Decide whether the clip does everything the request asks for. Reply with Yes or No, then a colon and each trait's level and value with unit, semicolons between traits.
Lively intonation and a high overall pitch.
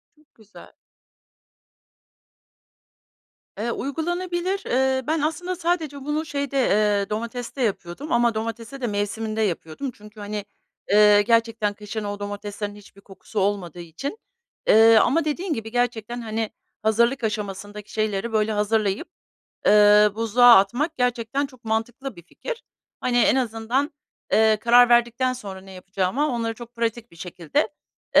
No: average, 4.0 semitones; high, 225 Hz